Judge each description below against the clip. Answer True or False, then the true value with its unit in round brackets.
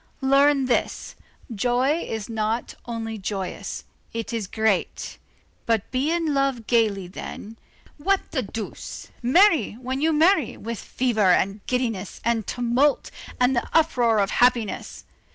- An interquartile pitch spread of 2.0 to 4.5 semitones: True (3.9 semitones)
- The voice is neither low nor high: False (235 Hz)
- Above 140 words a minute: False (135 wpm)